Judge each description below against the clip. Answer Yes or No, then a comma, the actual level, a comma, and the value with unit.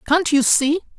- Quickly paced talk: No, average, 185 wpm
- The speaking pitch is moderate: No, very high, 310 Hz